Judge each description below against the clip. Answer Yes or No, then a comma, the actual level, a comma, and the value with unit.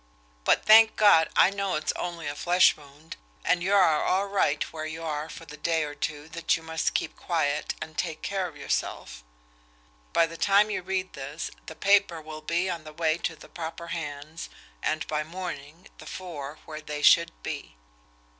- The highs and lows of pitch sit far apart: No, average, 2.9 semitones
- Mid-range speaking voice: Yes, medium, 160 Hz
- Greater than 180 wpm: Yes, average, 190 wpm